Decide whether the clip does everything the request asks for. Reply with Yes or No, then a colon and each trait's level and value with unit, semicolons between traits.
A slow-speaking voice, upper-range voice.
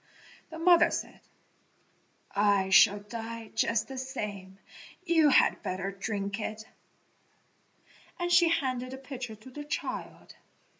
Yes: slow, 120 wpm; high, 230 Hz